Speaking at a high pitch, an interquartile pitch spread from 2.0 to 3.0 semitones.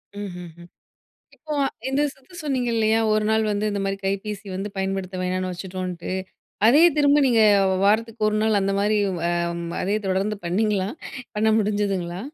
Yes: high, 205 Hz; average, 2.7 semitones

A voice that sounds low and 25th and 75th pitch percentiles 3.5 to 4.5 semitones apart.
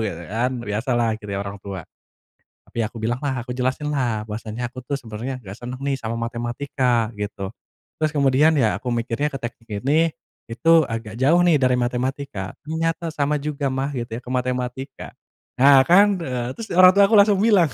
Yes: low, 125 Hz; average, 4.0 semitones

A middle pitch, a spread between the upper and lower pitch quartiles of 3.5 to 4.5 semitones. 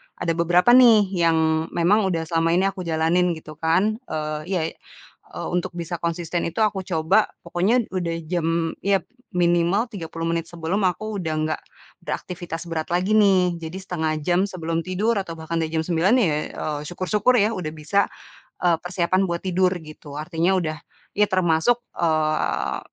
No: medium, 175 Hz; average, 2.7 semitones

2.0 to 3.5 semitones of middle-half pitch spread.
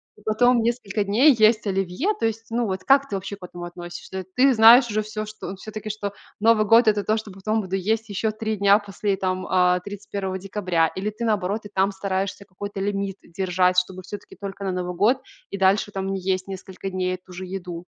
Yes: narrow, 2.4 semitones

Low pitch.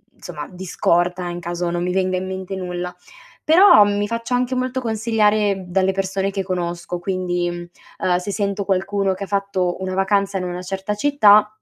No: high, 190 Hz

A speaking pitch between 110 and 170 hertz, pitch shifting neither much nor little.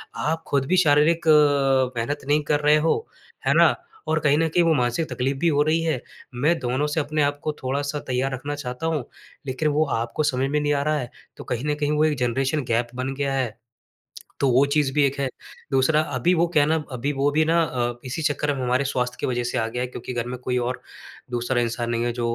Yes: medium, 140 Hz; average, 3.1 semitones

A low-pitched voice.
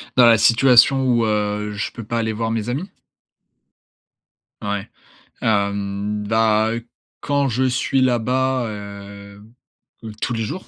Yes: low, 110 Hz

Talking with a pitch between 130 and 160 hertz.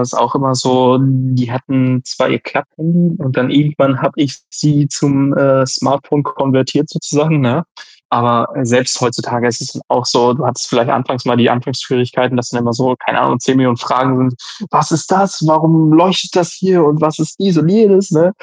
Yes: low, 135 Hz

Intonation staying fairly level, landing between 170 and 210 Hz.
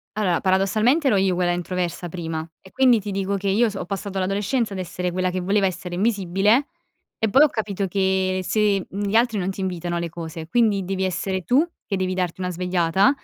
Yes: narrow, 2.3 semitones; high, 190 Hz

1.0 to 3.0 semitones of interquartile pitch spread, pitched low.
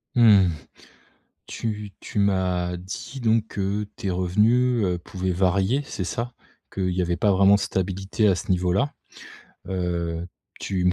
Yes: average, 2.7 semitones; very low, 95 Hz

